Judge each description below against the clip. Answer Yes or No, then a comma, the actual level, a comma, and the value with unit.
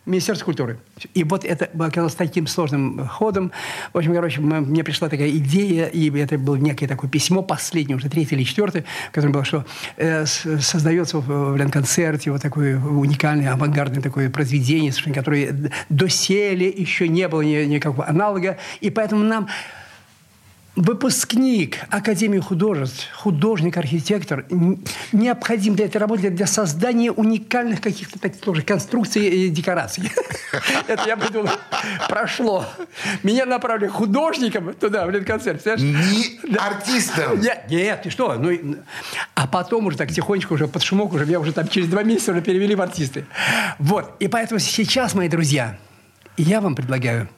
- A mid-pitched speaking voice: Yes, medium, 175 Hz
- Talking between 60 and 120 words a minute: No, average, 135 wpm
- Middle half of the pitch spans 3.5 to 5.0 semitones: No, wide, 5.5 semitones